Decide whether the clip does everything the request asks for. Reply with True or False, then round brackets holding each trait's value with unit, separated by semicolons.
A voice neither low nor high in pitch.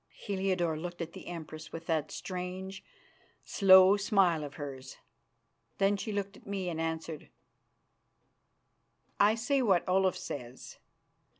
True (180 Hz)